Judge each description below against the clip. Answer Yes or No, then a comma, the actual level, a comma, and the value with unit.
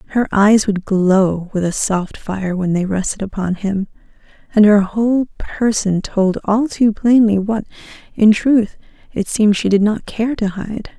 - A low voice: No, high, 205 Hz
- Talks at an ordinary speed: Yes, average, 175 wpm